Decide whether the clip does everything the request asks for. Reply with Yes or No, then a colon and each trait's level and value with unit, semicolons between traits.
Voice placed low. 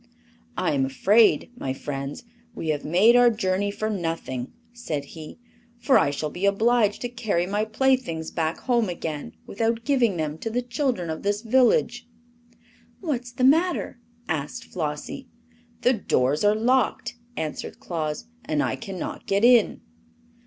No: high, 205 Hz